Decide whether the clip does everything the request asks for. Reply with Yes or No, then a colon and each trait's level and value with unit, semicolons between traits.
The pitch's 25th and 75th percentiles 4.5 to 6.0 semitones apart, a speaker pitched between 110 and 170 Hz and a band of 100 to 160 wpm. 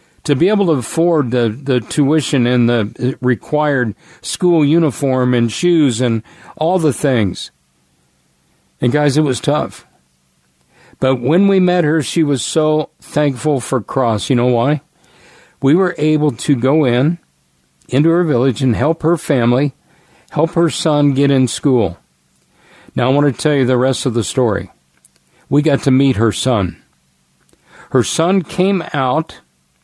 Yes: average, 4.8 semitones; low, 135 Hz; average, 155 wpm